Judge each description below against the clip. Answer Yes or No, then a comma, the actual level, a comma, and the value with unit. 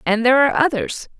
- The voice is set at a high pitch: Yes, very high, 255 Hz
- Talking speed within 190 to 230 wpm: Yes, average, 200 wpm